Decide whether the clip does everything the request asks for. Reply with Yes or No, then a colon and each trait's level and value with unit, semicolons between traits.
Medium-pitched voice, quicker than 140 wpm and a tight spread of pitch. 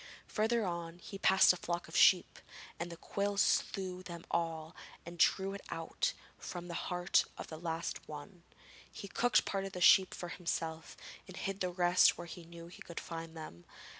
Yes: medium, 175 Hz; average, 195 wpm; narrow, 2.3 semitones